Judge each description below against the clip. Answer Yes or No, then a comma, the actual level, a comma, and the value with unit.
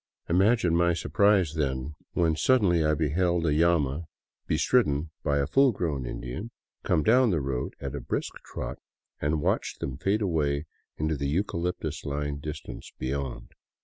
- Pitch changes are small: No, average, 3.7 semitones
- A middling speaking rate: Yes, average, 150 wpm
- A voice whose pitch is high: No, very low, 80 Hz